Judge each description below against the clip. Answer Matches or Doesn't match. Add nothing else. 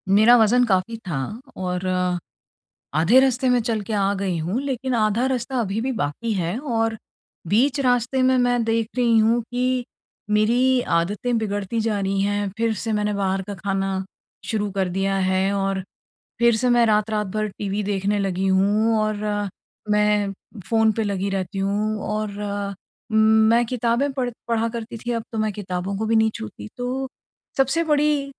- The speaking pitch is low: Doesn't match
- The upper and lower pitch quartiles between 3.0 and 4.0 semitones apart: Matches